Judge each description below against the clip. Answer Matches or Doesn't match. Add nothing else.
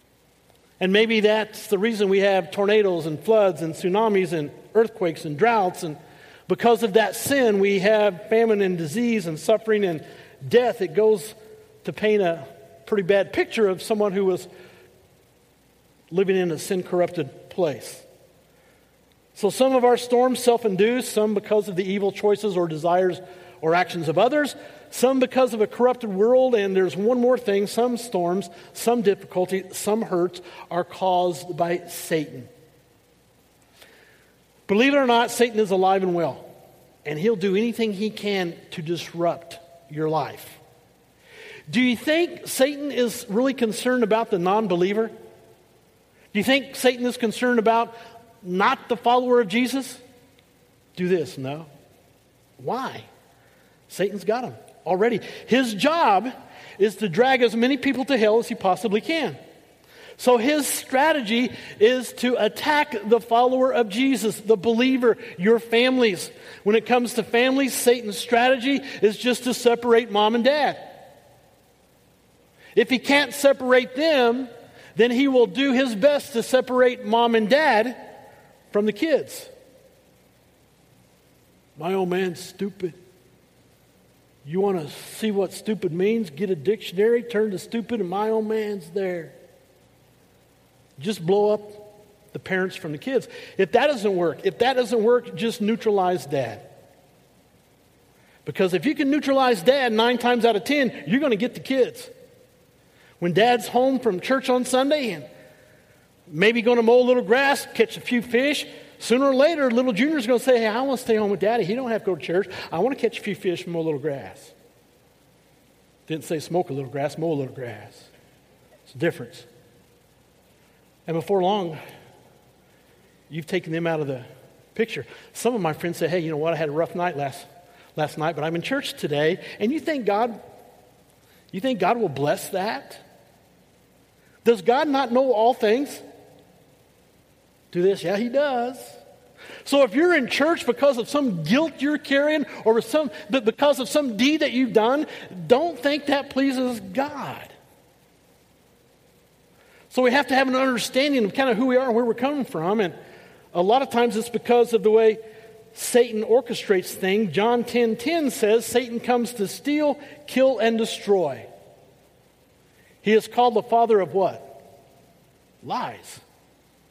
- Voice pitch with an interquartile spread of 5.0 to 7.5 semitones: Matches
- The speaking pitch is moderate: Doesn't match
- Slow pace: Doesn't match